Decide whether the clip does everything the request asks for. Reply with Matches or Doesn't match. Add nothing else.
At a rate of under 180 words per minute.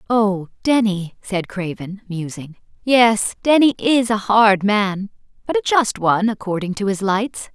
Matches